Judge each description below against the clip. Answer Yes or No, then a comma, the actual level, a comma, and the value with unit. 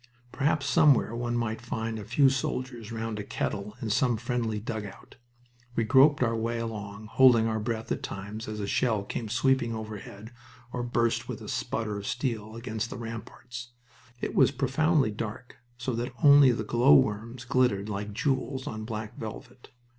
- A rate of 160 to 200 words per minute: Yes, average, 170 wpm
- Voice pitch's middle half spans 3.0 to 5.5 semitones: No, narrow, 2.6 semitones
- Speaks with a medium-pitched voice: No, low, 115 Hz